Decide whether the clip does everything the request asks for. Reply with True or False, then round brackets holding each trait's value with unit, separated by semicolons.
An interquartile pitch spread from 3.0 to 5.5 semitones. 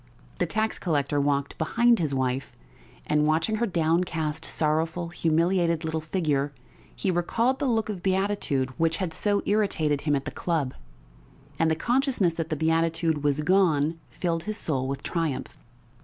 True (3.9 semitones)